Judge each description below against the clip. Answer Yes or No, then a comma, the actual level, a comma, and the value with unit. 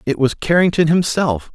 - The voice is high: No, medium, 160 Hz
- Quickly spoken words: No, average, 155 wpm